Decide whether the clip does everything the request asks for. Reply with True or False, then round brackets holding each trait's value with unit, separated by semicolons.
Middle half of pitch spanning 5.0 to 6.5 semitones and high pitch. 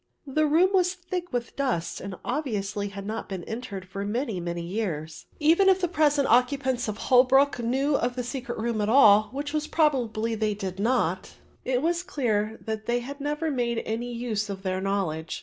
True (5.5 semitones; 235 Hz)